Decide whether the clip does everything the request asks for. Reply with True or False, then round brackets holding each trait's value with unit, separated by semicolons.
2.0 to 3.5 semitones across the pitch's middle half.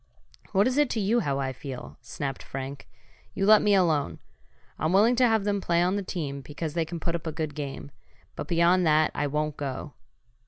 False (5.4 semitones)